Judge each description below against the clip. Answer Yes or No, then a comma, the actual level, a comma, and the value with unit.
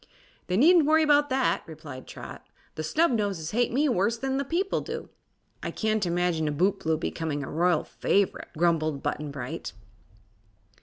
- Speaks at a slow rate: No, average, 155 wpm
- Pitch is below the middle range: No, medium, 185 Hz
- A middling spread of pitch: No, wide, 9.0 semitones